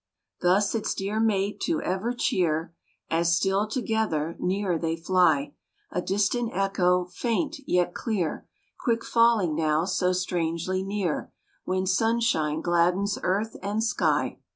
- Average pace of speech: No, slow, 130 wpm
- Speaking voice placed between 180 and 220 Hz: Yes, medium, 185 Hz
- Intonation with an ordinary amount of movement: Yes, average, 4.0 semitones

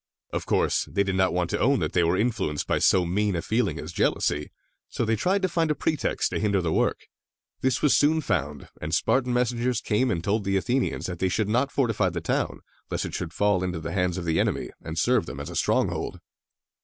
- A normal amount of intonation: No, wide, 5.9 semitones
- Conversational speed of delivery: No, fast, 235 wpm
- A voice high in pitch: No, low, 100 Hz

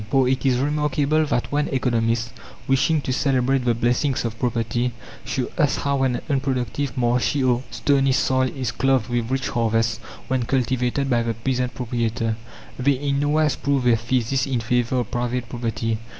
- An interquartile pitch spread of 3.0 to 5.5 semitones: No, narrow, 2.4 semitones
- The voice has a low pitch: Yes, low, 125 Hz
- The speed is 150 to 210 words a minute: Yes, average, 165 wpm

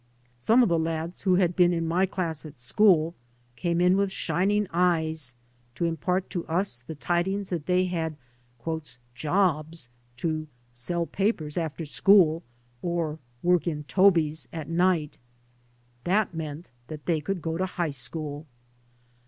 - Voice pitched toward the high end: No, medium, 165 Hz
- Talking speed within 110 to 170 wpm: Yes, average, 160 wpm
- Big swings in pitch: No, average, 2.8 semitones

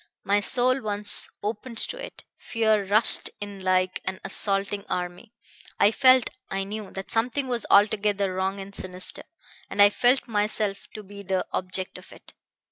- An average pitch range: No, narrow, 2.3 semitones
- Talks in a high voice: Yes, high, 205 Hz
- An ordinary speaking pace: Yes, average, 160 wpm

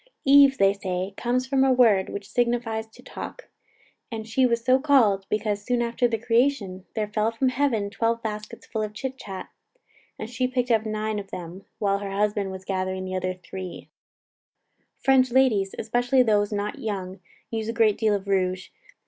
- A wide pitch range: No, average, 3.7 semitones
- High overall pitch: Yes, high, 220 Hz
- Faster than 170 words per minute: Yes, average, 180 wpm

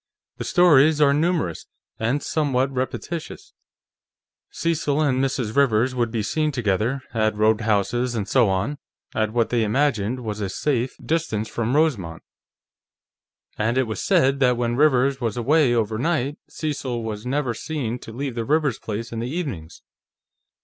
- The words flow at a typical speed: Yes, average, 155 wpm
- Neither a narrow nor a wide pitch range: Yes, average, 4.5 semitones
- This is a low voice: Yes, low, 125 Hz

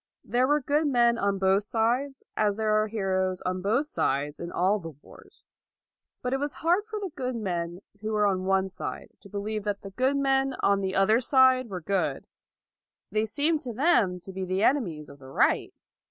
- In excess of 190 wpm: Yes, average, 200 wpm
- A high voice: Yes, high, 215 Hz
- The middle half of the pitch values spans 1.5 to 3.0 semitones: No, wide, 5.5 semitones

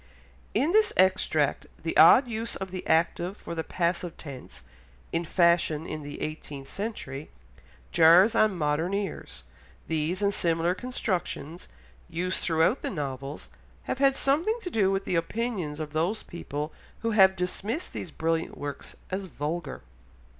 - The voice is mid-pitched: Yes, medium, 175 Hz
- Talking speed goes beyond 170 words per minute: No, average, 145 wpm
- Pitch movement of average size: Yes, average, 4.4 semitones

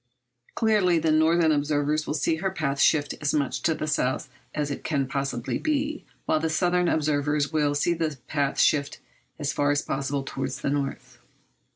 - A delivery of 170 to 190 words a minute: Yes, average, 180 wpm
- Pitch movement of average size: No, narrow, 2.3 semitones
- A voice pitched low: No, medium, 150 Hz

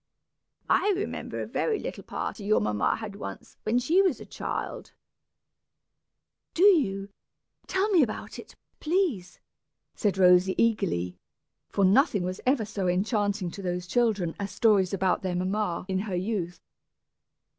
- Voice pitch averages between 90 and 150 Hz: No, high, 200 Hz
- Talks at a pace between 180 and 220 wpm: No, average, 145 wpm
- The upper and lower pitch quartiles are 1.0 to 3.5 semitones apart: No, average, 4.6 semitones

